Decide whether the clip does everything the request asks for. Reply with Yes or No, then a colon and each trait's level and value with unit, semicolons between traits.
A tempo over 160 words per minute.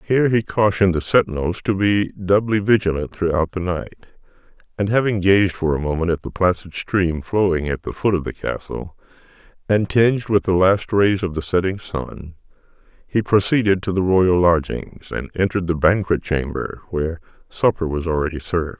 Yes: average, 175 wpm